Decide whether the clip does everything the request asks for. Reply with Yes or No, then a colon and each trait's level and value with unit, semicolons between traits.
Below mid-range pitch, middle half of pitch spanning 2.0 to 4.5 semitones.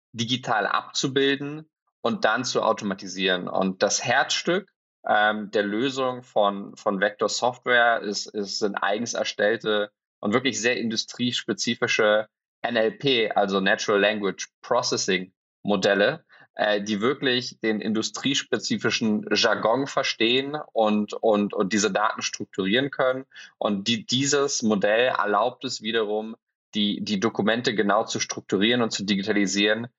Yes: low, 110 Hz; average, 3.3 semitones